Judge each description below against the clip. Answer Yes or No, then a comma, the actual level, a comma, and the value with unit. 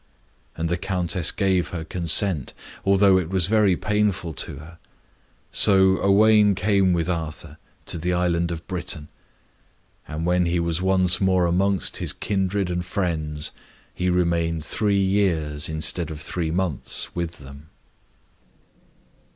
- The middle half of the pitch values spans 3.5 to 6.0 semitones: No, narrow, 2.6 semitones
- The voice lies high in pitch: No, very low, 90 Hz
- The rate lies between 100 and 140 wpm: Yes, slow, 135 wpm